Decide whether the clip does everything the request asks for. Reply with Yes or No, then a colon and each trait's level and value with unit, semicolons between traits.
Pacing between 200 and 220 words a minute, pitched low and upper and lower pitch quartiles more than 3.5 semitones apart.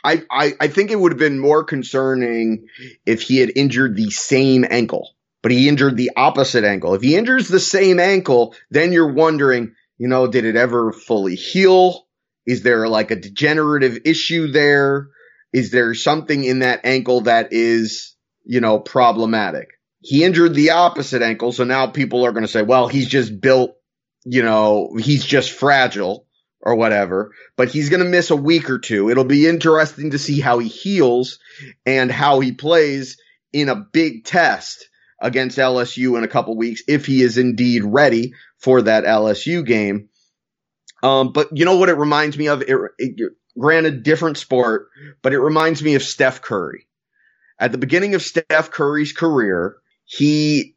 No: average, 175 wpm; low, 130 Hz; average, 4.2 semitones